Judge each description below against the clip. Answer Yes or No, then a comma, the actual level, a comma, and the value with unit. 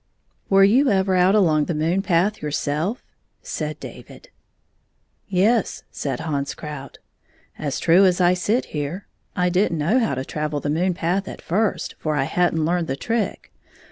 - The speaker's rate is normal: Yes, average, 190 wpm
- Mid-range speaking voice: Yes, medium, 175 Hz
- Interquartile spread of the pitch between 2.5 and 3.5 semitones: No, average, 4.3 semitones